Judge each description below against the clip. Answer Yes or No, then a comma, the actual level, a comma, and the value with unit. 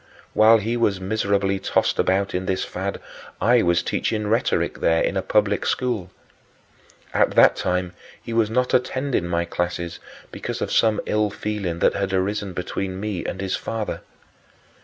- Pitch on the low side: Yes, low, 100 Hz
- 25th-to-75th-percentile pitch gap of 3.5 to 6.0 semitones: No, average, 2.9 semitones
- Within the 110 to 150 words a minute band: No, average, 160 wpm